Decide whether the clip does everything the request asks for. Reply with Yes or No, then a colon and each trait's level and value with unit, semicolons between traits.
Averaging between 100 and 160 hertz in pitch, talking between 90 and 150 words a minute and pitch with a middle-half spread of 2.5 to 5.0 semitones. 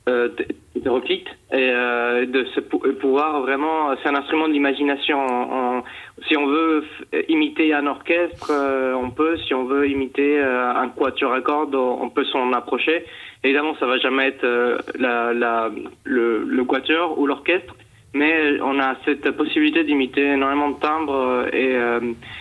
Yes: low, 135 Hz; slow, 145 wpm; average, 3.2 semitones